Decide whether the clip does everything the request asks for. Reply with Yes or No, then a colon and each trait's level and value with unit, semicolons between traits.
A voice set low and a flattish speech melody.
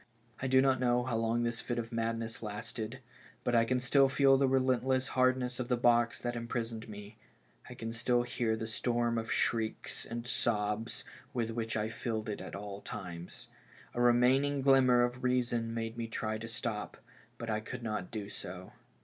Yes: low, 120 Hz; narrow, 1.8 semitones